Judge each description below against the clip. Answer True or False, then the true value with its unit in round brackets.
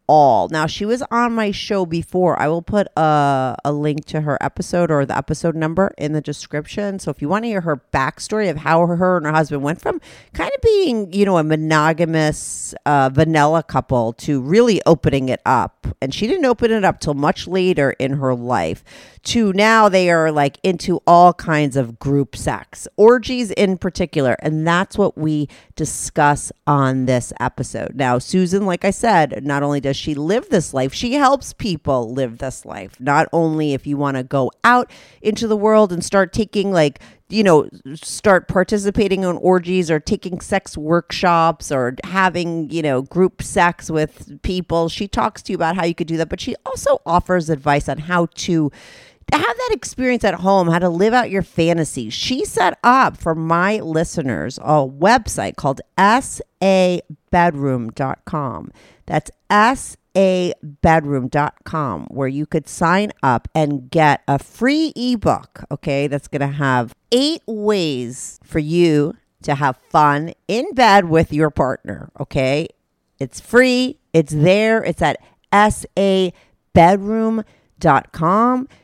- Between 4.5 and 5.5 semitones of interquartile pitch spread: True (5.2 semitones)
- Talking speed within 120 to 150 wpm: False (165 wpm)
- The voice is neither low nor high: True (165 Hz)